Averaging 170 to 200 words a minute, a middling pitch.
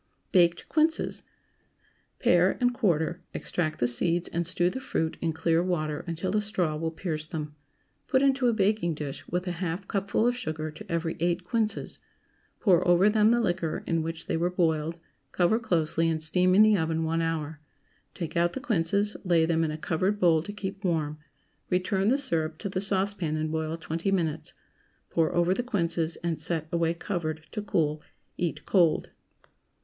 Yes: average, 180 wpm; medium, 170 Hz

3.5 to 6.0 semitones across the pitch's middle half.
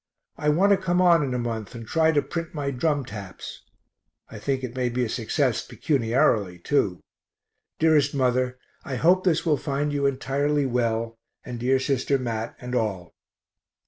Yes: average, 4.1 semitones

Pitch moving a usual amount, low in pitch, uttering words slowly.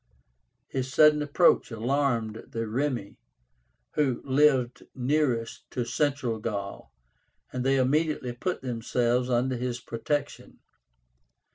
Yes: average, 3.3 semitones; low, 125 Hz; slow, 105 wpm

